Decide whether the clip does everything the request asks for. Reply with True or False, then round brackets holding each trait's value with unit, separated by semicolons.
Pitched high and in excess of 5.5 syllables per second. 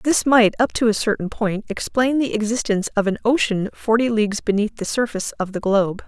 True (220 Hz; 5.8 syllables/s)